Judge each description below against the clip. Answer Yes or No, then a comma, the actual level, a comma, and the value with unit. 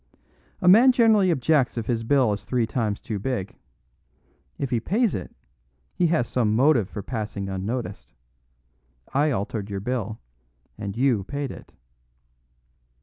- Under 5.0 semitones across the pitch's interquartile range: No, wide, 5.5 semitones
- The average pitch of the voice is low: Yes, low, 120 Hz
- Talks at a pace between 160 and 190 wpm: No, average, 145 wpm